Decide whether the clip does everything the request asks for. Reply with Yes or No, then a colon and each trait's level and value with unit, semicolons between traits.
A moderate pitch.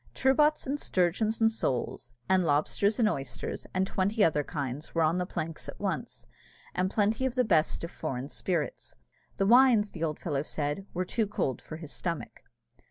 Yes: medium, 180 Hz